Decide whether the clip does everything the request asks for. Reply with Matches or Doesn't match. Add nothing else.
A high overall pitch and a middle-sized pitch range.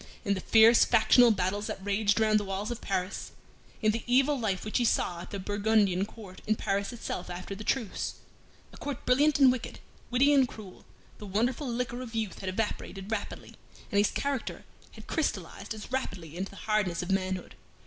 Matches